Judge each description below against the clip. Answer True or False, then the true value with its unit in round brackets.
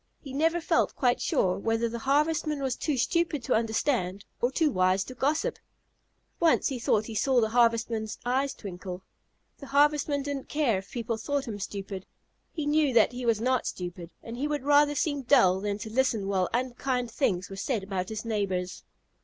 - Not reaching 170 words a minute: False (185 wpm)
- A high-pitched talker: True (240 Hz)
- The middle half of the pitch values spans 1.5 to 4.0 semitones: False (5.6 semitones)